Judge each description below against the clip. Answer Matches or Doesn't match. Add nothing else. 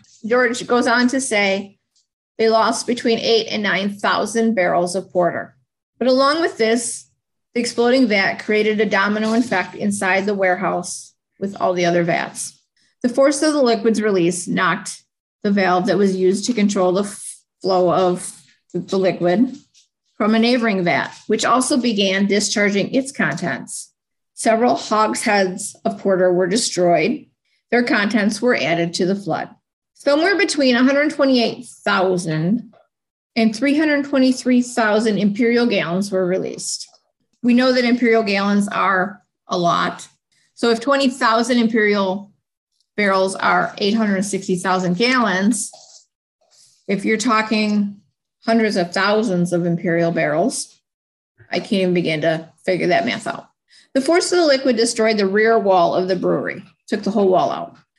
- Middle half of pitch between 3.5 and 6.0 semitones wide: Matches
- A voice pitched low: Doesn't match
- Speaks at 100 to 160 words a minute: Matches